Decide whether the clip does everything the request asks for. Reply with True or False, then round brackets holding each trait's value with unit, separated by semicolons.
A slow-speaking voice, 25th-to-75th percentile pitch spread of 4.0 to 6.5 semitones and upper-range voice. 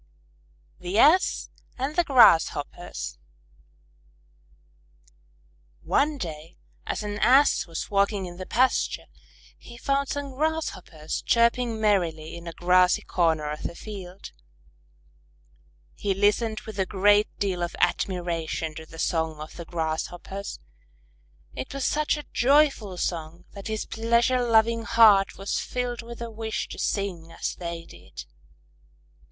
True (130 wpm; 5.6 semitones; 200 Hz)